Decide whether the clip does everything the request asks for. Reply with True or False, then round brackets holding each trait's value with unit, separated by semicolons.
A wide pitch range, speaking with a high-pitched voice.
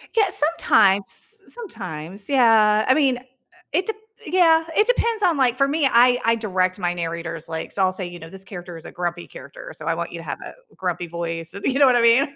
True (8.1 semitones; 210 Hz)